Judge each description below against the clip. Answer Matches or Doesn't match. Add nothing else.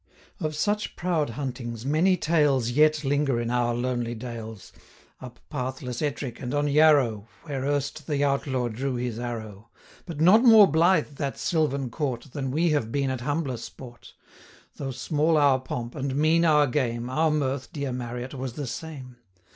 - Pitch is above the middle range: Doesn't match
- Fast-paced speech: Doesn't match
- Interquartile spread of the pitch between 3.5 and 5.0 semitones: Matches